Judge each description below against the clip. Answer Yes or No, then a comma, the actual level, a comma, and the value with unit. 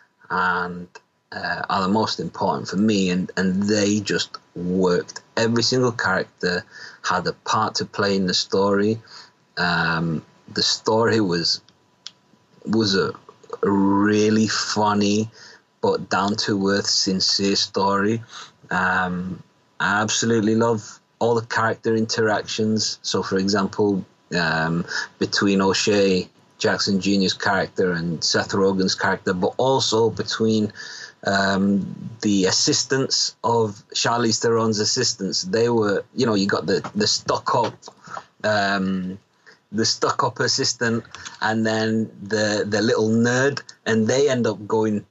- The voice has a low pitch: Yes, low, 105 Hz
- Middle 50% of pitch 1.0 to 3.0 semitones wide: Yes, narrow, 2.5 semitones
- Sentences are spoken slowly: Yes, slow, 125 wpm